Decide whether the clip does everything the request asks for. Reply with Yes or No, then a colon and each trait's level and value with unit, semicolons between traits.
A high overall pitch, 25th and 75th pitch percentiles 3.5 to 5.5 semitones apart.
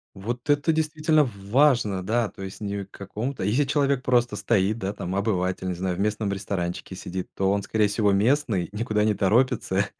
No: low, 105 Hz; average, 4.2 semitones